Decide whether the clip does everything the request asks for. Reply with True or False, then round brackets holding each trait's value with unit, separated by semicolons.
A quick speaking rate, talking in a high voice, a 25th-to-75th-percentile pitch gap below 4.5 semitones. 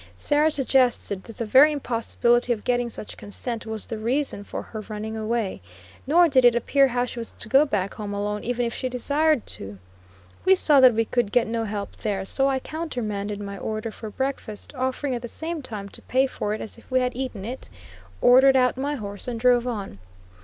True (210 wpm; 240 Hz; 3.6 semitones)